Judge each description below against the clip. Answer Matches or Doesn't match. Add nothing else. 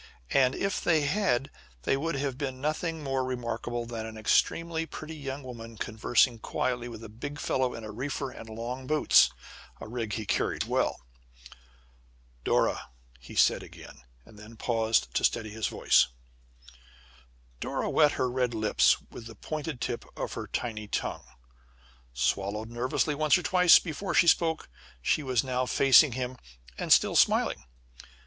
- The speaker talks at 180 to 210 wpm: Doesn't match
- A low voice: Matches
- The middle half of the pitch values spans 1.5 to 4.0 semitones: Doesn't match